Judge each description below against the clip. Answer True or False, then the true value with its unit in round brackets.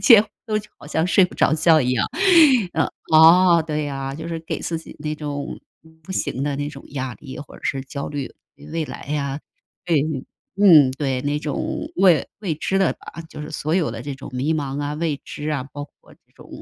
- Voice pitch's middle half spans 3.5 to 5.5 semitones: False (2.6 semitones)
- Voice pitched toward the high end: False (150 Hz)